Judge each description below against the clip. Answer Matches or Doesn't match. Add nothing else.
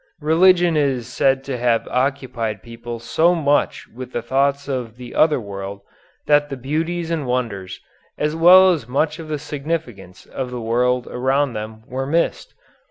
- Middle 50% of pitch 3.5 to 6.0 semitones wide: Matches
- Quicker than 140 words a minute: Matches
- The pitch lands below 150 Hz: Matches